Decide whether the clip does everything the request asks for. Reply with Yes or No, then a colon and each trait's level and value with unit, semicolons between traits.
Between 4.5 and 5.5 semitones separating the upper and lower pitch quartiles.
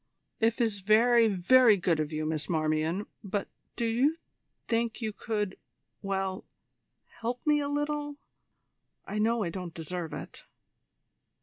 Yes: average, 4.8 semitones